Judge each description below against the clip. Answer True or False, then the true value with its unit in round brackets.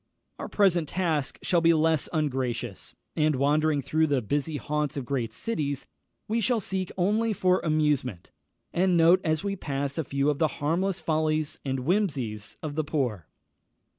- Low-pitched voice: False (155 Hz)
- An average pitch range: True (3.8 semitones)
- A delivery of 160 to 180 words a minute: True (165 wpm)